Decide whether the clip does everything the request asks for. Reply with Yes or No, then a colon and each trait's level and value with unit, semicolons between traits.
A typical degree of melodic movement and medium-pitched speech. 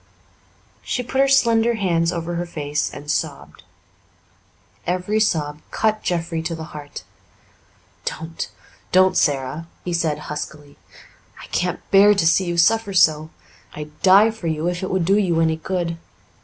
Yes: average, 3.6 semitones; medium, 170 Hz